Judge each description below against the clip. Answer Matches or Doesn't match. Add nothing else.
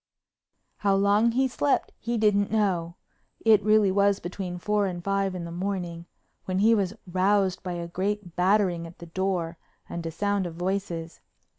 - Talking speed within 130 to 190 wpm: Matches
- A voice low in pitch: Doesn't match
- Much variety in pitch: Doesn't match